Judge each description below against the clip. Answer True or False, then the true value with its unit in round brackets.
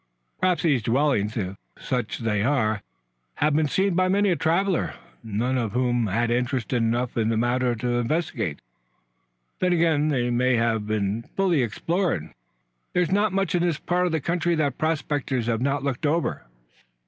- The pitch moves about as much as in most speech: False (6.4 semitones)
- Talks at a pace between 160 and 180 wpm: True (170 wpm)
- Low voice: True (130 Hz)